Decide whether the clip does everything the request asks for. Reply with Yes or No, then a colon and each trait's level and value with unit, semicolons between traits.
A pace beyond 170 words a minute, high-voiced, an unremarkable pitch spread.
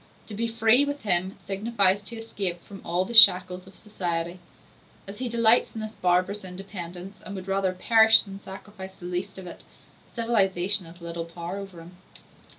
Yes: average, 180 wpm; high, 195 Hz; average, 3.2 semitones